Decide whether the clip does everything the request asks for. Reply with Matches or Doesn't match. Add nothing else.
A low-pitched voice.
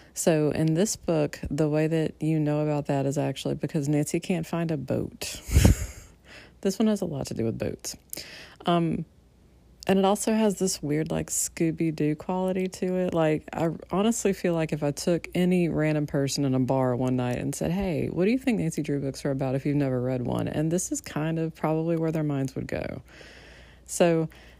Doesn't match